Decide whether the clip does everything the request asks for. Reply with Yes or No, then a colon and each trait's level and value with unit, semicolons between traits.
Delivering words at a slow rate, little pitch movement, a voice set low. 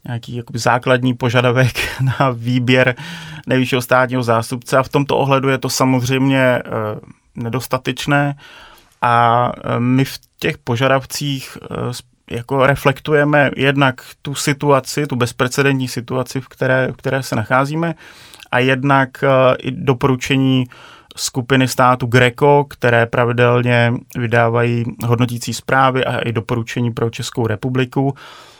Yes: slow, 110 wpm; narrow, 1.9 semitones; low, 130 Hz